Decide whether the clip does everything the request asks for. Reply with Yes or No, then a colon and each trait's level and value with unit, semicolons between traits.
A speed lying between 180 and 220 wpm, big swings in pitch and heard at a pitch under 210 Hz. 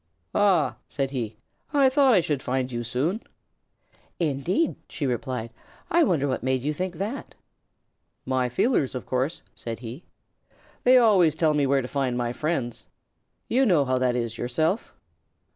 No: average, 160 wpm; wide, 6.3 semitones; medium, 140 Hz